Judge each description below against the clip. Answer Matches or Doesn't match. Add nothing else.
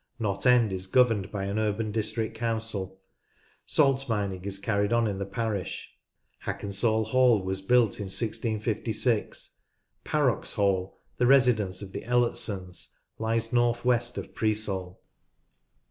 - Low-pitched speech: Matches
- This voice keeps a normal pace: Doesn't match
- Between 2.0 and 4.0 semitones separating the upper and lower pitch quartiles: Matches